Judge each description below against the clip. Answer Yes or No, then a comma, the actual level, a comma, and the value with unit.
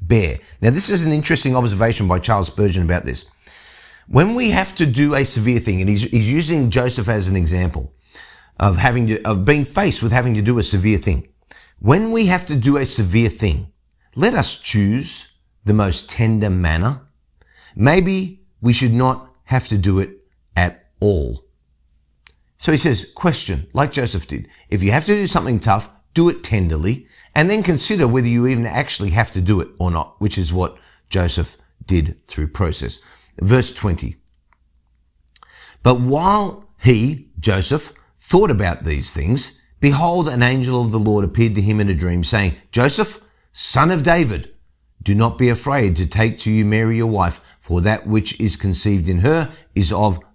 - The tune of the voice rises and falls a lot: Yes, wide, 6.2 semitones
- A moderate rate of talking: Yes, average, 180 wpm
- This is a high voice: No, low, 110 Hz